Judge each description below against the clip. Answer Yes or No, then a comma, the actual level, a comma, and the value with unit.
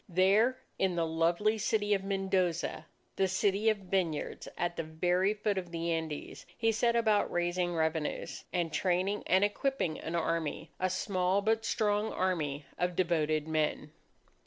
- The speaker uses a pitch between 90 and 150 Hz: No, medium, 185 Hz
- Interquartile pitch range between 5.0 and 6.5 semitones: No, average, 3.7 semitones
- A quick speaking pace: No, average, 155 wpm